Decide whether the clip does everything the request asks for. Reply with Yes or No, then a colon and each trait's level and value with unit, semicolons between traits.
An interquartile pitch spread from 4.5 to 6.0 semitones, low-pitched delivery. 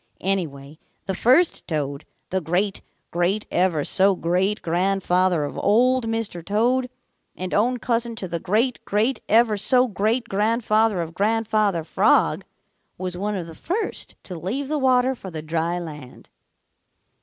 No: average, 4.8 semitones; high, 195 Hz